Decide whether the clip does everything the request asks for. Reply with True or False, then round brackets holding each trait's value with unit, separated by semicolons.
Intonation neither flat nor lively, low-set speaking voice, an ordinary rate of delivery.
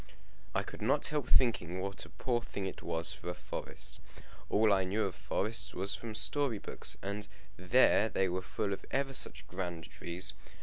True (4.1 semitones; 100 Hz; 185 wpm)